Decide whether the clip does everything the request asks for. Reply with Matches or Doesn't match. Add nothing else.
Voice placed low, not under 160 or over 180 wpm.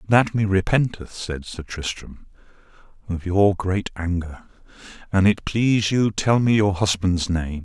Doesn't match